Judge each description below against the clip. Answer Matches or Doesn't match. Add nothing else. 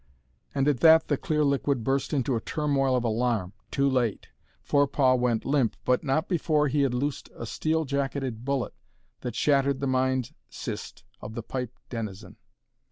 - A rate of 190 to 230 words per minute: Doesn't match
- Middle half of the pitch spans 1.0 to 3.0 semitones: Matches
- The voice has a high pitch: Doesn't match